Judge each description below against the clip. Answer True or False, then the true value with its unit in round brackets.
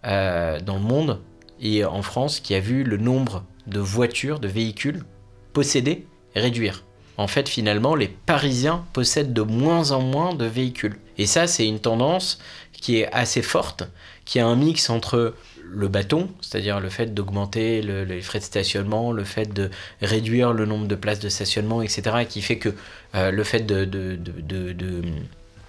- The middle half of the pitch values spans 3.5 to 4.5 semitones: True (3.9 semitones)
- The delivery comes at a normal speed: True (180 wpm)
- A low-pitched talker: True (110 Hz)